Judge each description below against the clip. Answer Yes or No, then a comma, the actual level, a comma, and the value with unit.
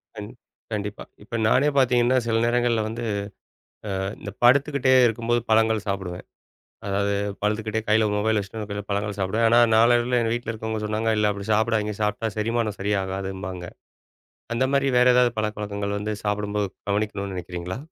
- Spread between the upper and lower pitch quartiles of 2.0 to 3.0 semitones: Yes, narrow, 2.4 semitones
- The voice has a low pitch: Yes, low, 110 Hz